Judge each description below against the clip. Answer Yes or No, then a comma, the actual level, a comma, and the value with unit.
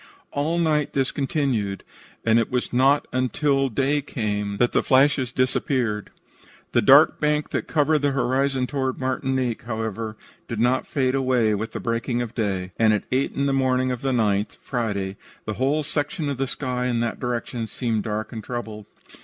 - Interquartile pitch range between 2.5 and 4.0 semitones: Yes, average, 3.5 semitones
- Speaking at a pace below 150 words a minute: No, average, 180 wpm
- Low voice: Yes, low, 125 Hz